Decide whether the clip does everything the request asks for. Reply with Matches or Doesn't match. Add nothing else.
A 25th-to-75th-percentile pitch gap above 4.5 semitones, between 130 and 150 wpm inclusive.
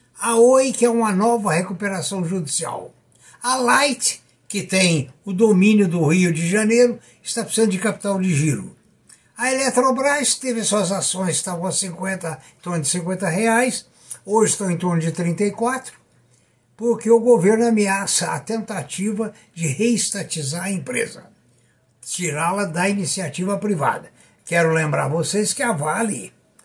Matches